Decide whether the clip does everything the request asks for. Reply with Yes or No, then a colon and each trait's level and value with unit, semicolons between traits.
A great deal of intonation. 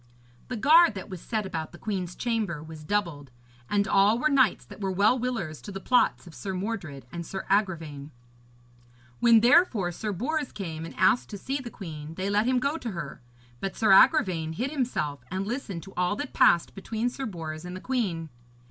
Yes: wide, 5.8 semitones